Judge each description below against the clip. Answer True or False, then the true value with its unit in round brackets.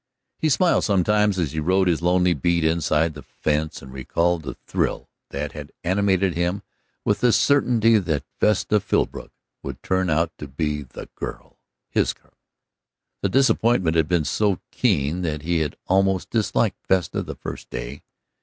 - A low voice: True (85 Hz)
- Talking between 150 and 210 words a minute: True (165 wpm)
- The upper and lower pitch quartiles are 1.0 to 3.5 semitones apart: False (4.2 semitones)